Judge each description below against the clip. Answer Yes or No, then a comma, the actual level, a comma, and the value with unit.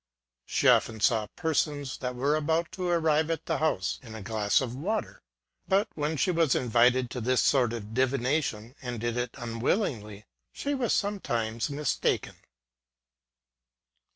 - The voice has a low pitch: Yes, low, 130 Hz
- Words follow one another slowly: No, average, 155 wpm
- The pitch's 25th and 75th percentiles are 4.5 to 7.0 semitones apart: Yes, wide, 5.5 semitones